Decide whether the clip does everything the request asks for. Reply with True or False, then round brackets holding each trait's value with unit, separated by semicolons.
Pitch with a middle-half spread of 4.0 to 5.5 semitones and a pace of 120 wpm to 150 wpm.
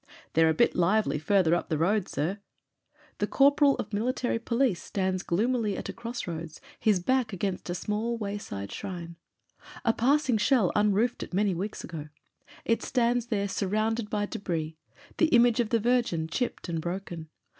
False (5.1 semitones; 175 wpm)